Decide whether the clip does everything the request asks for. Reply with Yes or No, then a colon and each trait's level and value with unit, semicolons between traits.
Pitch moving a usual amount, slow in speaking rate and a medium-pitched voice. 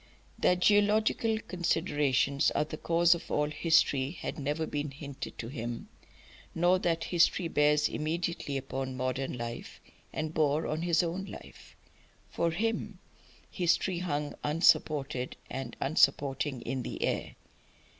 Yes: average, 3.9 semitones; slow, 130 wpm; medium, 150 Hz